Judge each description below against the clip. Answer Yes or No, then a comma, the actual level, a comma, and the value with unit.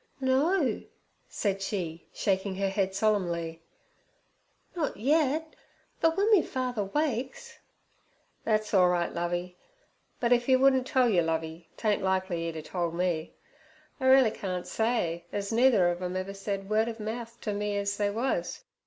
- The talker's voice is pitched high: Yes, high, 205 Hz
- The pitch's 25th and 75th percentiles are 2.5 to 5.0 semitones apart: No, wide, 5.6 semitones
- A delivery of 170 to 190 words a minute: No, average, 155 wpm